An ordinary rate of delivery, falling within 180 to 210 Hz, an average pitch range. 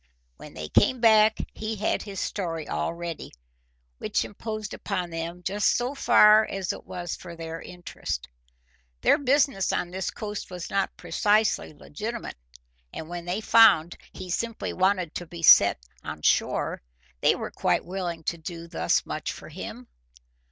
Yes: average, 160 wpm; medium, 185 Hz; average, 4.1 semitones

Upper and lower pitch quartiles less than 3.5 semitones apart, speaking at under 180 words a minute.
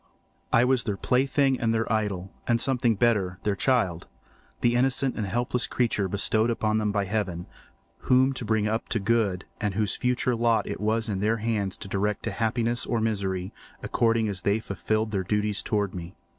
No: average, 2.9 semitones; average, 185 wpm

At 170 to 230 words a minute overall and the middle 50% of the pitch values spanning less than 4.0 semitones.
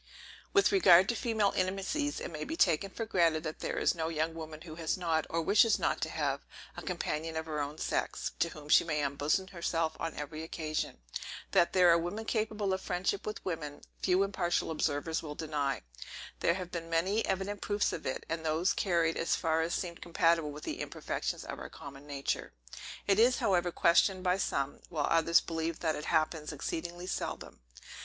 Yes: average, 195 wpm; average, 3.1 semitones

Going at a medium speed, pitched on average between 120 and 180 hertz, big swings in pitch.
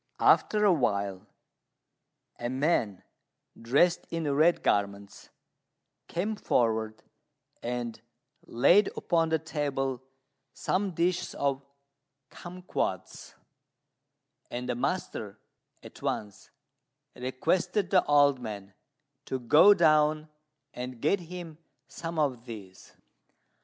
No: slow, 95 wpm; medium, 140 Hz; wide, 6.3 semitones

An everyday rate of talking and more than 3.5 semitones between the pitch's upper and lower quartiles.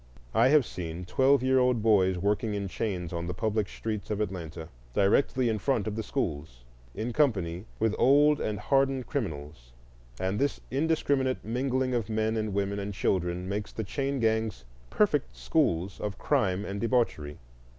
Yes: average, 165 wpm; wide, 5.4 semitones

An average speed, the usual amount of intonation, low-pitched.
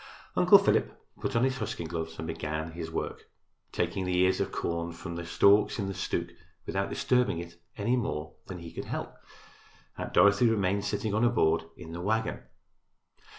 Yes: average, 185 wpm; average, 4.0 semitones; very low, 90 Hz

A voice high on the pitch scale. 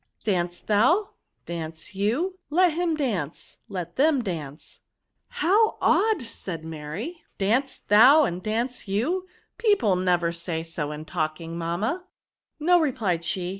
Yes: high, 205 Hz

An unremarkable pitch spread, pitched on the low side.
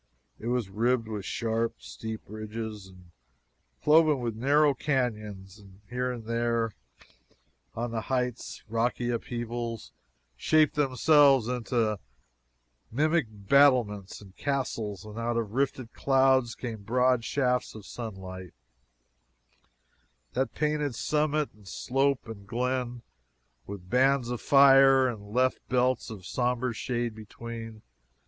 Yes: average, 3.3 semitones; low, 120 Hz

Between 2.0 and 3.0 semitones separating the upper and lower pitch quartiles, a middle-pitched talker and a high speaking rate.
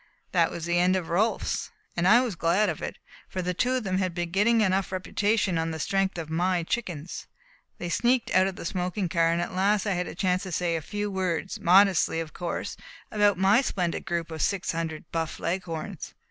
Yes: average, 2.7 semitones; medium, 180 Hz; fast, 215 wpm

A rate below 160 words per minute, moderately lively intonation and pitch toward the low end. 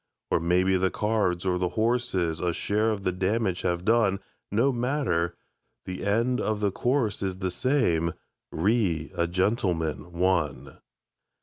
Yes: average, 145 wpm; average, 4.2 semitones; very low, 95 Hz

